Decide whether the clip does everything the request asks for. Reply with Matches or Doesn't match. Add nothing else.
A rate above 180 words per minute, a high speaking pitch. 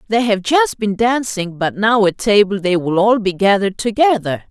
Matches